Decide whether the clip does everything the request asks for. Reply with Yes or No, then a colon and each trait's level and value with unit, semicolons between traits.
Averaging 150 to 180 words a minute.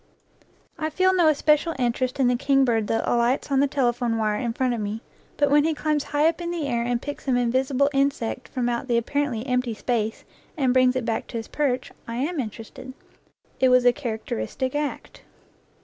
No: fast, 205 wpm